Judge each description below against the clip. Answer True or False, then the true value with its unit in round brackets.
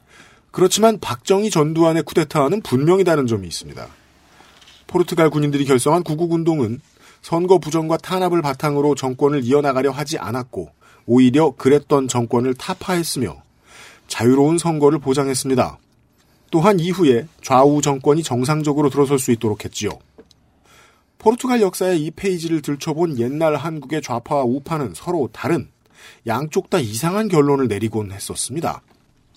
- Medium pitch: True (145 Hz)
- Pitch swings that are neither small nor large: True (4.8 semitones)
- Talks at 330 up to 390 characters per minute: True (340 characters per minute)